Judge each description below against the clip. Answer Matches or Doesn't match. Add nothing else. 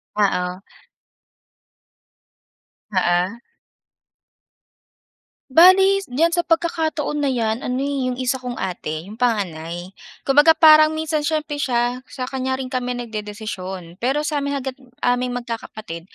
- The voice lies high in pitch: Matches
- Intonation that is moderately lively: Doesn't match